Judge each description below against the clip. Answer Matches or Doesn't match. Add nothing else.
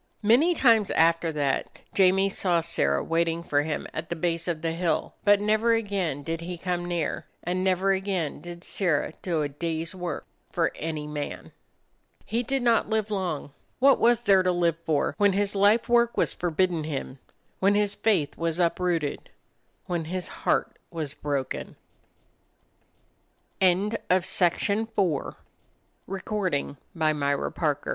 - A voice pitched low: Doesn't match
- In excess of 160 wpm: Doesn't match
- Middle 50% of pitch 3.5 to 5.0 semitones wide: Matches